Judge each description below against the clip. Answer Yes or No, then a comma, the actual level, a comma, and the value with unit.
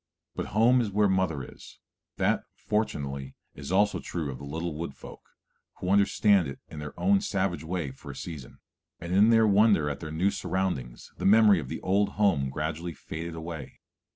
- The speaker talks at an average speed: Yes, average, 185 wpm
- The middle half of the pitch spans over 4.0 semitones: Yes, average, 5.3 semitones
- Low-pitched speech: Yes, very low, 85 Hz